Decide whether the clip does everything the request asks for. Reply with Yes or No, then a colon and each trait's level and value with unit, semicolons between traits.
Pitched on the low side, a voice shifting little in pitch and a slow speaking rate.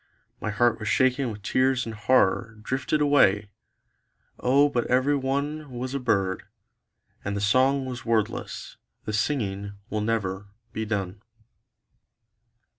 No: low, 115 Hz; average, 4.3 semitones; slow, 130 wpm